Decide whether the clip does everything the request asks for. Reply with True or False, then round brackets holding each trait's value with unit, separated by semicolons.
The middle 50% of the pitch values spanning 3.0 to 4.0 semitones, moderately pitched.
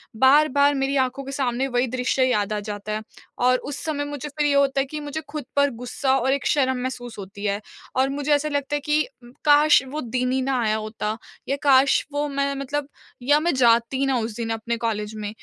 False (3.5 semitones; 265 Hz)